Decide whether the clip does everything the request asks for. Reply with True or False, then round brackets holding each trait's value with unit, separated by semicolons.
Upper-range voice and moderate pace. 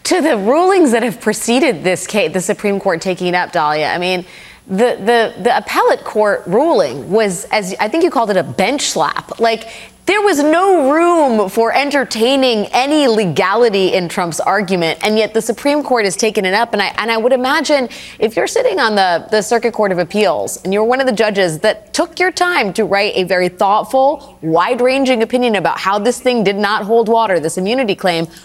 False (220 Hz; 210 wpm)